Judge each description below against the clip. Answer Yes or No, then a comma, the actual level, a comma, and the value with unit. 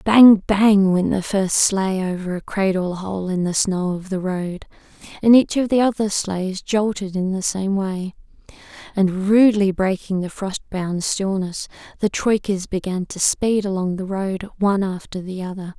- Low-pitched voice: No, high, 195 Hz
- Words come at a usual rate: Yes, average, 175 wpm